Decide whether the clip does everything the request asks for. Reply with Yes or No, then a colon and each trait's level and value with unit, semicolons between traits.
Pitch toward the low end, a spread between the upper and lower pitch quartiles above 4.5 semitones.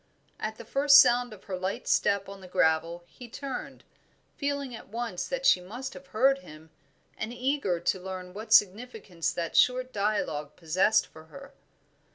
No: high, 210 Hz; wide, 5.6 semitones